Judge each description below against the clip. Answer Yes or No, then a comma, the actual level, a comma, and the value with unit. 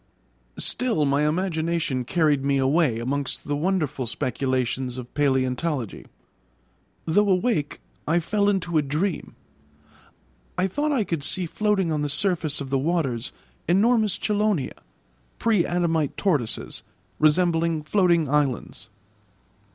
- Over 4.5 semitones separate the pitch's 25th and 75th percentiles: Yes, average, 4.9 semitones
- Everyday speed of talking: No, slow, 120 wpm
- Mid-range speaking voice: Yes, medium, 160 Hz